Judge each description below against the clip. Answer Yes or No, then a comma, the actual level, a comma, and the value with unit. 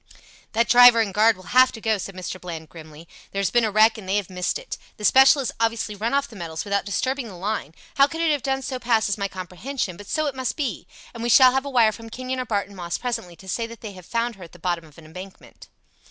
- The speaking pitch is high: Yes, high, 220 Hz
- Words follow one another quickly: Yes, fast, 270 wpm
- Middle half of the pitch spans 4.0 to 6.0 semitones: Yes, average, 5.0 semitones